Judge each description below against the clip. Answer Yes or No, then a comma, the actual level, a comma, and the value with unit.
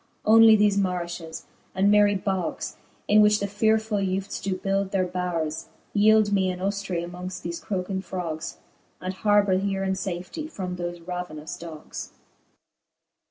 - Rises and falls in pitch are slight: Yes, narrow, 2.3 semitones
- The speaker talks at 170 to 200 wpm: No, average, 145 wpm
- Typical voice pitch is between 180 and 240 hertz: Yes, high, 190 Hz